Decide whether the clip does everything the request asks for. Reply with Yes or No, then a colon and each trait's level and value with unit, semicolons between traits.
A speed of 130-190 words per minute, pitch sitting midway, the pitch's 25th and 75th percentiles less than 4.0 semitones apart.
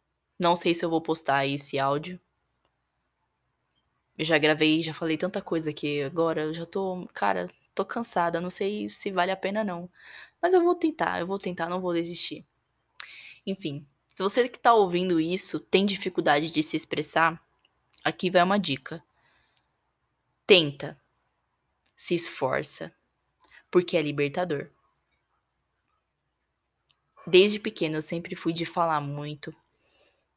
Yes: average, 140 wpm; medium, 165 Hz; average, 3.6 semitones